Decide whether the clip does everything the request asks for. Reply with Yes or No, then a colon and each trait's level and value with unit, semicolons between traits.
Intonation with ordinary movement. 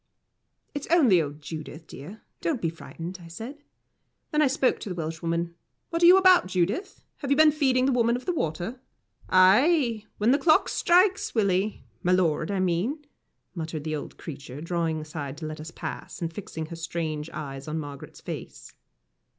No: wide, 8.6 semitones